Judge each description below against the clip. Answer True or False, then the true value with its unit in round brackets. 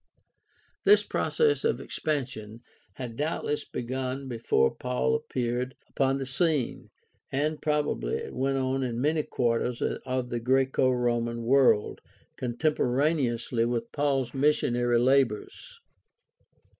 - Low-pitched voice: True (130 Hz)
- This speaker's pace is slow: True (110 wpm)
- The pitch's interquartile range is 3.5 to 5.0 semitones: False (2.8 semitones)